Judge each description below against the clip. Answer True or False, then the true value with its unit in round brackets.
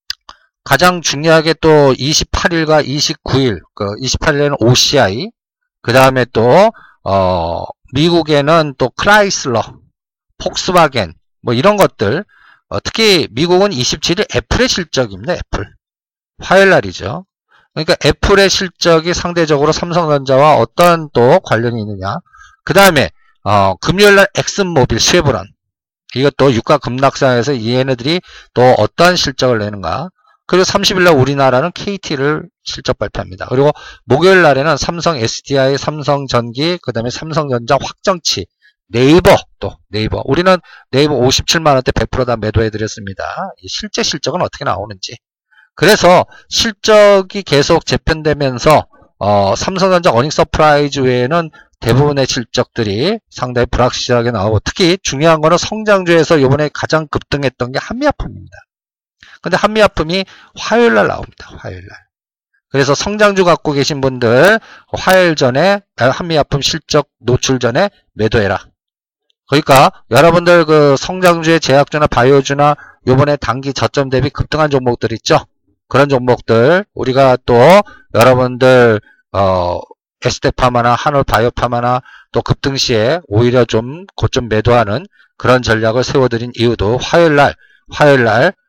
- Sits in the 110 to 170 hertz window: True (140 Hz)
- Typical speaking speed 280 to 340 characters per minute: True (305 characters per minute)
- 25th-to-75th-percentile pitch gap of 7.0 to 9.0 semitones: False (6.1 semitones)